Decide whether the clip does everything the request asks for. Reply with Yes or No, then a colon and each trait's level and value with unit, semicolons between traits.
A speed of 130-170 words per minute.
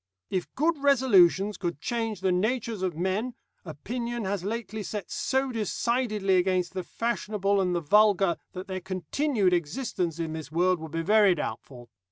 Yes: average, 160 wpm